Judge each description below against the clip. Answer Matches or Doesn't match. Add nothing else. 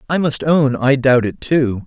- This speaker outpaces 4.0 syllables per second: Matches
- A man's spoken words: Matches